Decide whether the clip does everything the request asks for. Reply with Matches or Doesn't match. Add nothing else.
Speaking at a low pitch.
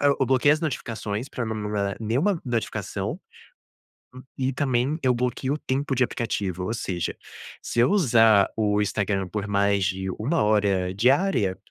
Matches